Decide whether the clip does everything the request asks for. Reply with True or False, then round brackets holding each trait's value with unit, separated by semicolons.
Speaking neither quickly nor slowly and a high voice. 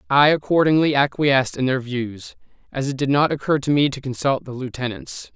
False (190 wpm; 135 Hz)